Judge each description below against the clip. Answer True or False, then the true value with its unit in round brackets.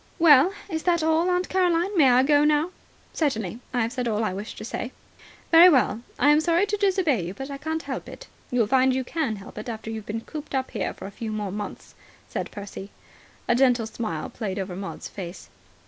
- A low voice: False (260 Hz)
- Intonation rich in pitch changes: True (6.9 semitones)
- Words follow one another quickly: True (215 wpm)